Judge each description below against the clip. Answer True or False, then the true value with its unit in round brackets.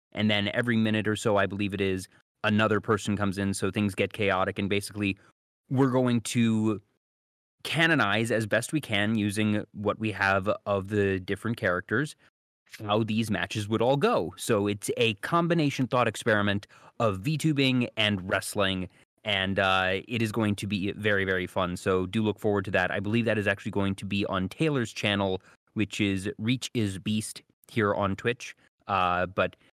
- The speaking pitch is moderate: False (105 Hz)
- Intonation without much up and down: True (2.2 semitones)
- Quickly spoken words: False (180 wpm)